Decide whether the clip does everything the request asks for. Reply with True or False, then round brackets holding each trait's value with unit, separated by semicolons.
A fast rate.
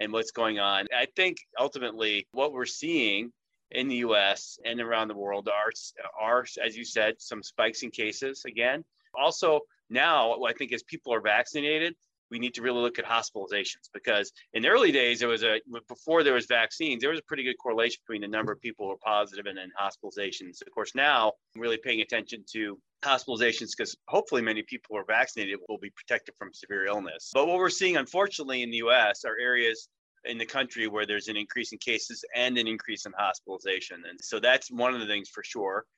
True (210 wpm)